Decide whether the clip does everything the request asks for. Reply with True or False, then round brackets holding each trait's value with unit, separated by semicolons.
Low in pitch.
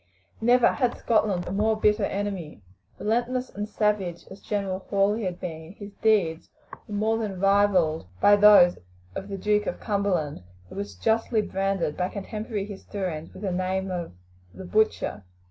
False (200 Hz)